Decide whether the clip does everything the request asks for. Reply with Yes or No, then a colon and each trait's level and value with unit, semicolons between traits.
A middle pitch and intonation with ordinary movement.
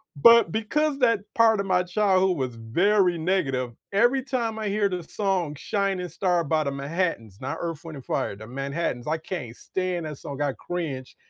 No: medium, 175 Hz; wide, 6.2 semitones